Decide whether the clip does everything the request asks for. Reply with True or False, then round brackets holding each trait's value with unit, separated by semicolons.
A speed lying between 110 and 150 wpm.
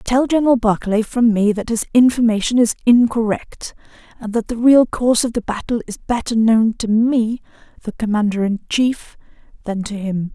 False (175 wpm)